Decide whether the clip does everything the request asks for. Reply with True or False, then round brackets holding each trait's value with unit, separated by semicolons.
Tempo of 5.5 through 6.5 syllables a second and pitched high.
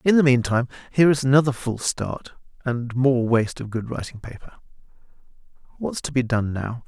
False (5.8 syllables/s; 125 Hz)